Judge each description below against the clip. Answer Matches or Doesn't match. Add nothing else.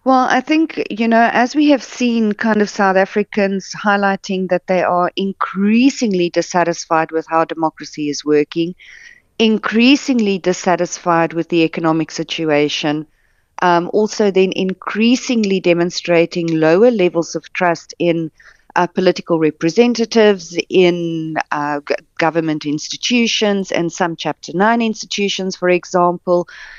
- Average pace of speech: Doesn't match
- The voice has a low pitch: Doesn't match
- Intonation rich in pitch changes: Doesn't match